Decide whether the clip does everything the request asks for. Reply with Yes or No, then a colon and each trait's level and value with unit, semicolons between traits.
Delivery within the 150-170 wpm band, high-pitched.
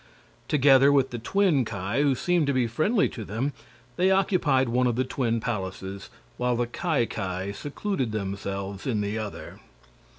No: average, 165 wpm; low, 125 Hz